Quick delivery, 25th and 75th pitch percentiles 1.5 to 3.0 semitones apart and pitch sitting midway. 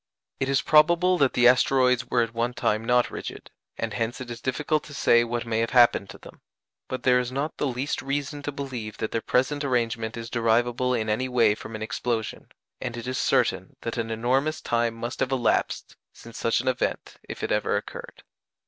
No: fast, 210 wpm; narrow, 2.4 semitones; low, 120 Hz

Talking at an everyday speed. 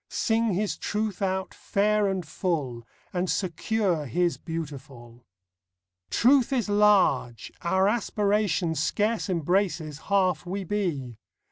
No: slow, 110 wpm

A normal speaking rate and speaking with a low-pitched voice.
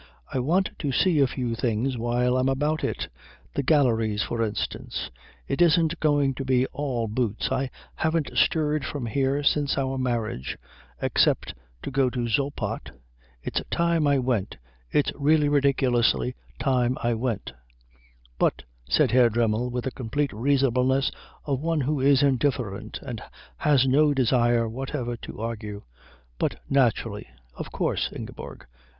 Yes: average, 145 wpm; low, 130 Hz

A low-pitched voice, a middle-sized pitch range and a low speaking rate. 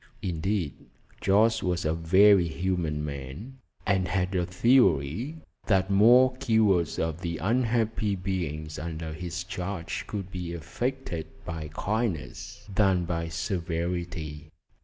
Yes: very low, 90 Hz; average, 3.8 semitones; slow, 115 wpm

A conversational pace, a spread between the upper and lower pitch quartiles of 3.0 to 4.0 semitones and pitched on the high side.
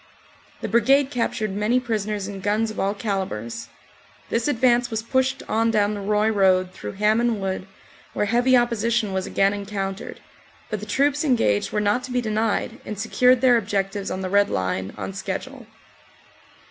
Yes: average, 170 wpm; average, 3.4 semitones; high, 210 Hz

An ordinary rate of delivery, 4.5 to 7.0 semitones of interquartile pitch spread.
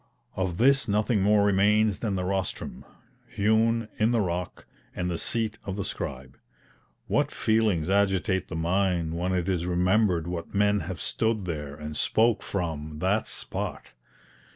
No: average, 155 wpm; average, 3.5 semitones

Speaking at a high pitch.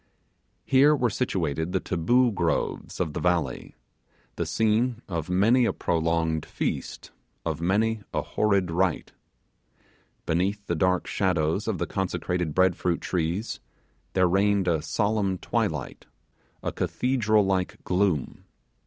No: very low, 95 Hz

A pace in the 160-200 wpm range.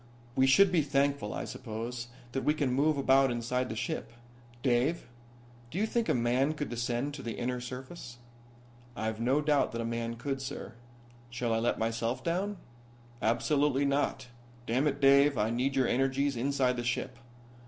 Yes: average, 175 wpm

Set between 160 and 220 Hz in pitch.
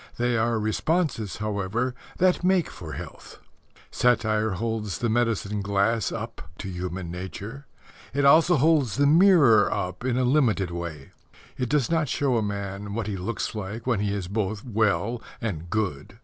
No: low, 110 Hz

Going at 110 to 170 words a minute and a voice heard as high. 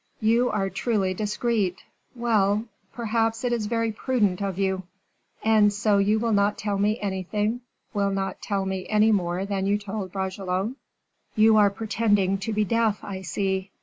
Yes: average, 165 wpm; high, 205 Hz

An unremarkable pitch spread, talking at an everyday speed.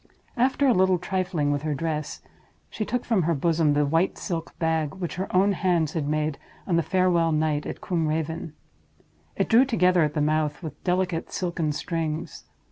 Yes: average, 3.2 semitones; average, 185 wpm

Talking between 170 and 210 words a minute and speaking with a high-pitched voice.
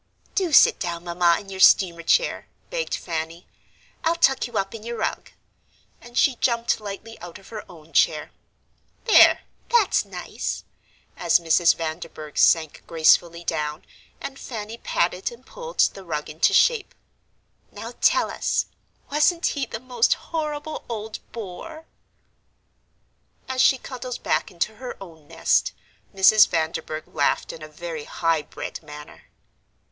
No: average, 140 wpm; high, 195 Hz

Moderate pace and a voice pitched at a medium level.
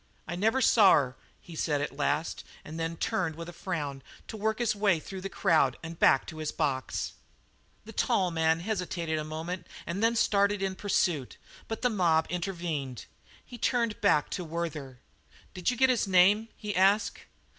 Yes: average, 180 wpm; medium, 175 Hz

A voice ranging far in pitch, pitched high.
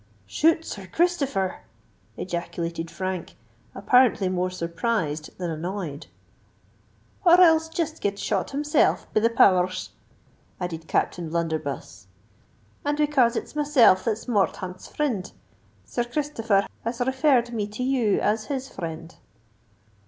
Yes: wide, 7.0 semitones; high, 210 Hz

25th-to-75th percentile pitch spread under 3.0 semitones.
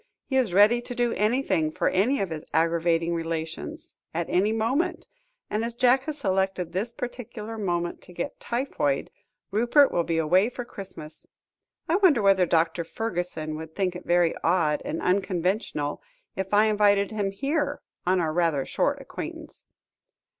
No: wide, 5.5 semitones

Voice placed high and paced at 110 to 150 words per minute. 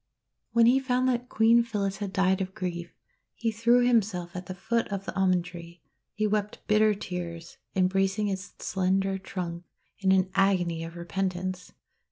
No: high, 195 Hz; average, 165 wpm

